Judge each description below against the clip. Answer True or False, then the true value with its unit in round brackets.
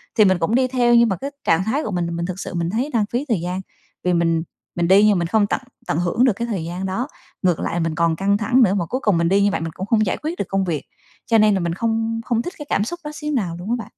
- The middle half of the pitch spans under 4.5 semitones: False (5.1 semitones)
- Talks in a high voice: True (200 Hz)